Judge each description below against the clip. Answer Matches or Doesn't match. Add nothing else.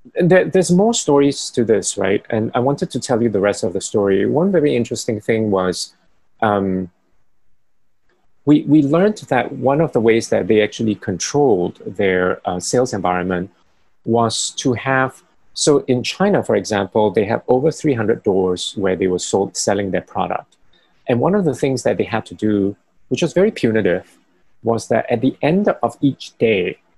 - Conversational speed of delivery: Matches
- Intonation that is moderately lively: Doesn't match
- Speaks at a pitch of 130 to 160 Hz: Doesn't match